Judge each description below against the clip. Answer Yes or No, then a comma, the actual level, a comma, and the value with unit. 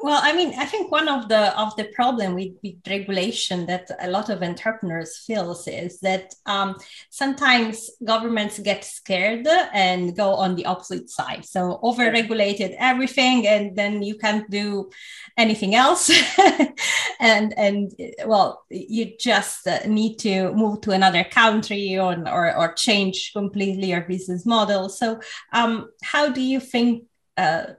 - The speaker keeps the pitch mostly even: No, average, 3.8 semitones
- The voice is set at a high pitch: Yes, high, 210 Hz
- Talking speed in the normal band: Yes, average, 150 wpm